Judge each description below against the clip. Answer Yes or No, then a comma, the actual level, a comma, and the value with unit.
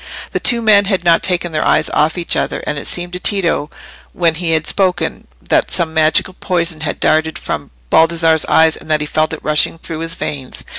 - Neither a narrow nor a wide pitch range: No, narrow, 2.2 semitones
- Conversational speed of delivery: No, fast, 210 wpm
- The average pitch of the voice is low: No, medium, 165 Hz